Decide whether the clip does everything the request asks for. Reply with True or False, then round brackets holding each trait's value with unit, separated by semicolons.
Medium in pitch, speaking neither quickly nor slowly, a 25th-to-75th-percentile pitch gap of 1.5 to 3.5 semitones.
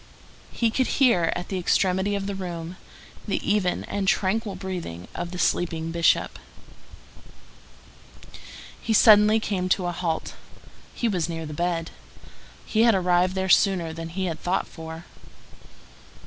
True (180 Hz; 145 wpm; 2.9 semitones)